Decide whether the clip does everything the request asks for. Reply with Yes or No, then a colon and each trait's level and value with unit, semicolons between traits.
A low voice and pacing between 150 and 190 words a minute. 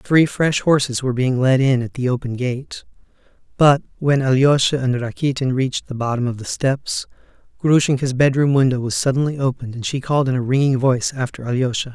Yes: low, 130 Hz; average, 185 wpm